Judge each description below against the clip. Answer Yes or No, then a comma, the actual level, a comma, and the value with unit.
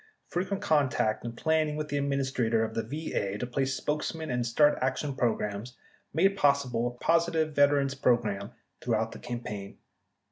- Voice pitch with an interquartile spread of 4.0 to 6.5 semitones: Yes, average, 4.4 semitones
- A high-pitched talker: No, low, 135 Hz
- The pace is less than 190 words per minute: Yes, average, 165 wpm